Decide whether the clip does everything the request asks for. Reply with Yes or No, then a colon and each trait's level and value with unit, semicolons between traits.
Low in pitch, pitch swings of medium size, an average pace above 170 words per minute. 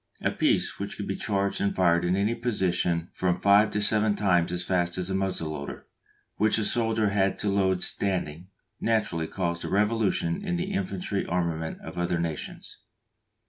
Yes: very low, 95 Hz; average, 3.6 semitones; average, 180 wpm